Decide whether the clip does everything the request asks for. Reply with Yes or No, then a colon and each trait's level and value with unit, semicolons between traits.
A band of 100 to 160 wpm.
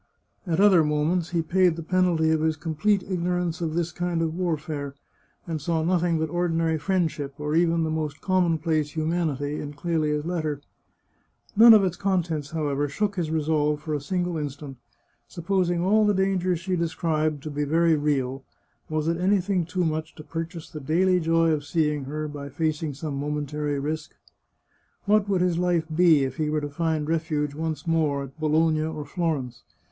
No: average, 180 wpm